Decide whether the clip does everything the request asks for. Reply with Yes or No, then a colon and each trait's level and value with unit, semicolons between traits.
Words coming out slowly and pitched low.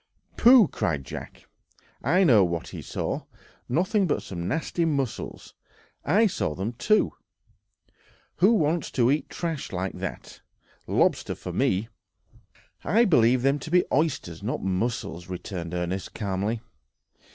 Yes: slow, 130 wpm; low, 120 Hz